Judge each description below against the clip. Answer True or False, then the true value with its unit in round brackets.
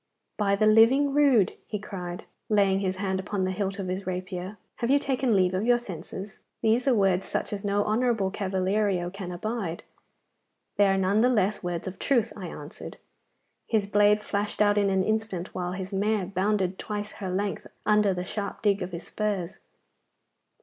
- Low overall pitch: False (200 Hz)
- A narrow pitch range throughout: True (2.2 semitones)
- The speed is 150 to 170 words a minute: False (185 wpm)